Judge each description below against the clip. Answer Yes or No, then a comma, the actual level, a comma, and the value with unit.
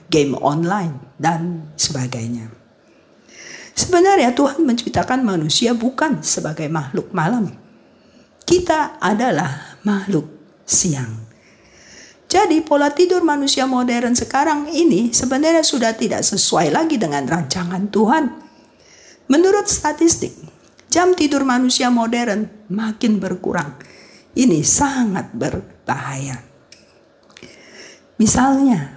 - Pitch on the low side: No, high, 235 Hz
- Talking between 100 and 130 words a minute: No, average, 90 wpm